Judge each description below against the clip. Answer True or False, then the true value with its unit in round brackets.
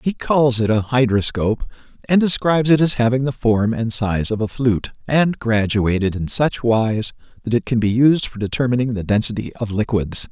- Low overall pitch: True (120 Hz)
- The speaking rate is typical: True (190 wpm)